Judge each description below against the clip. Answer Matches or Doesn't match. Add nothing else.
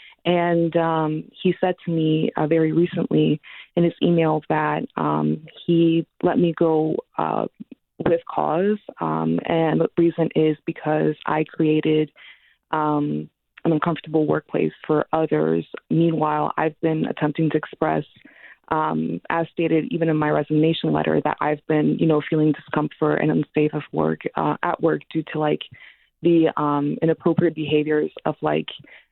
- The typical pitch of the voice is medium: Matches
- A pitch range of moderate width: Doesn't match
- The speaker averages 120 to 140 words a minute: Doesn't match